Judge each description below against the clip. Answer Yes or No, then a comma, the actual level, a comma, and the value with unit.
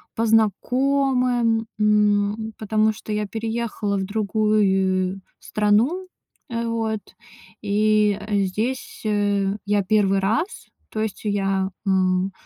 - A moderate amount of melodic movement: No, narrow, 2.0 semitones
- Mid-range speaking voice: No, high, 210 Hz